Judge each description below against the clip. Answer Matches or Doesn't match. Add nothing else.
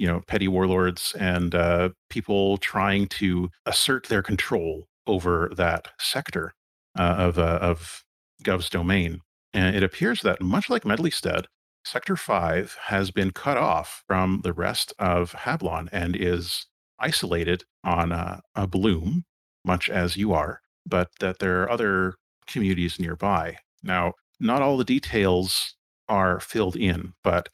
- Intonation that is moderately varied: Doesn't match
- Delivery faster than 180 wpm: Doesn't match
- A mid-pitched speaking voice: Doesn't match